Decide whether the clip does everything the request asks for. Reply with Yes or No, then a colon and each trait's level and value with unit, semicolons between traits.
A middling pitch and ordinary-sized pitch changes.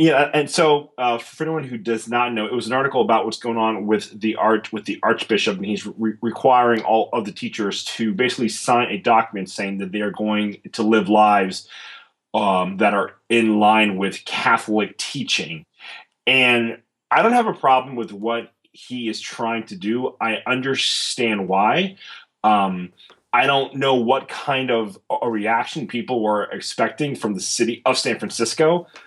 No: low, 115 Hz; average, 3.0 semitones